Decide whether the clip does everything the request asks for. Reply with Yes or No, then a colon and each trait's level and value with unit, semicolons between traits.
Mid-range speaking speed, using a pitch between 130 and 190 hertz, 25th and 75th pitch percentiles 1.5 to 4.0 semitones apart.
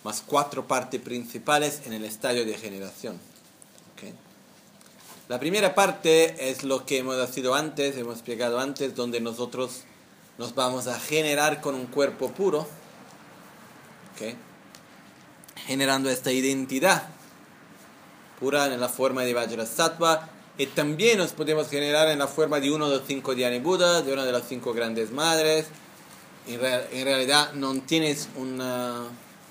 Yes: average, 145 wpm; low, 135 Hz; average, 3.4 semitones